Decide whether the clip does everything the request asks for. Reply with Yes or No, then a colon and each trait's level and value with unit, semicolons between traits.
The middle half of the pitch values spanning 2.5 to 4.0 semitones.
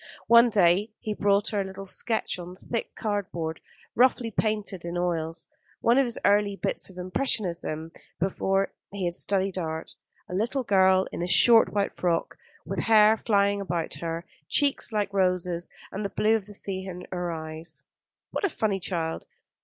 Yes: average, 3.3 semitones